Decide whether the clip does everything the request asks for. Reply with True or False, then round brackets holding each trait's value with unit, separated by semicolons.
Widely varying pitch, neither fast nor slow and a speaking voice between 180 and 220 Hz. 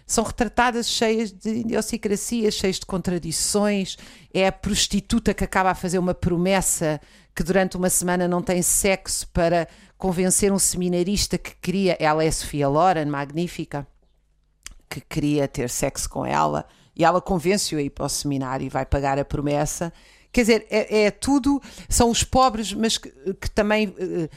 False (4.9 semitones; 165 wpm; 185 Hz)